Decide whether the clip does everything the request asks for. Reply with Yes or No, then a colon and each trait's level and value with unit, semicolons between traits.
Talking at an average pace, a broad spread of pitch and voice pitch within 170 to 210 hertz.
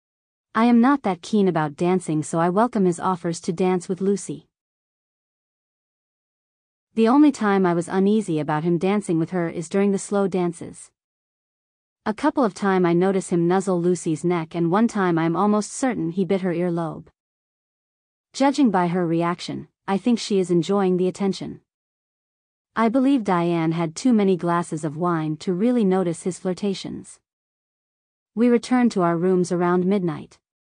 No: average, 165 wpm; average, 2.9 semitones; medium, 185 Hz